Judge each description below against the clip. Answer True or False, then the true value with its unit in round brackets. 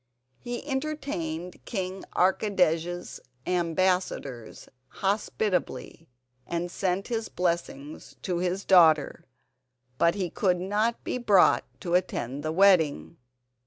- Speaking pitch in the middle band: True (180 Hz)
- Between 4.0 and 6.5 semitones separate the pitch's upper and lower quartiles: False (2.9 semitones)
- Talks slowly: True (100 wpm)